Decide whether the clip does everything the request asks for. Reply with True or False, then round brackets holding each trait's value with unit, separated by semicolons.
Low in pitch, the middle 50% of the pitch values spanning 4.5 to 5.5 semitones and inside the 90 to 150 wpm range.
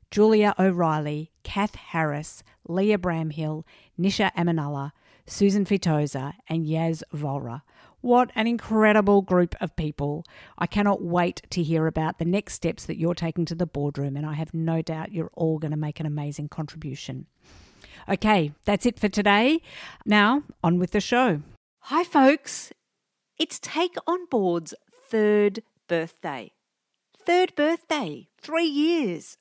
False (175 Hz; 5.1 semitones; 140 wpm)